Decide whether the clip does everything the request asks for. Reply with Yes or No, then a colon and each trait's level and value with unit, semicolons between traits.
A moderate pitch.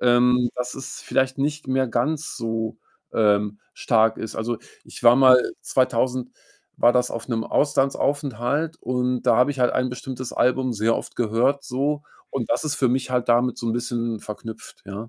No: low, 125 Hz